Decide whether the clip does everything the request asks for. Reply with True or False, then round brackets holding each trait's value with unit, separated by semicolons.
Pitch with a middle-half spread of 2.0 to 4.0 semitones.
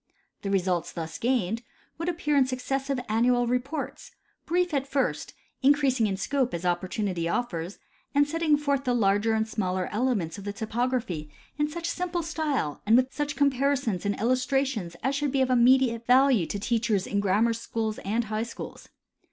False (5.3 semitones)